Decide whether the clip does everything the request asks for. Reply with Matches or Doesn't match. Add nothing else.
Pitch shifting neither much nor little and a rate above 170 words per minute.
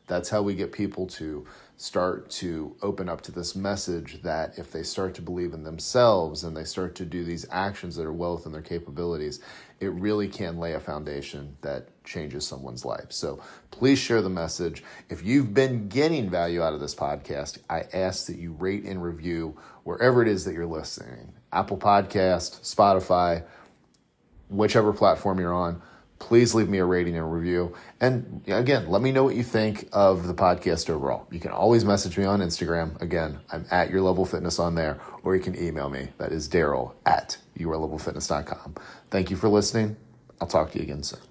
Matches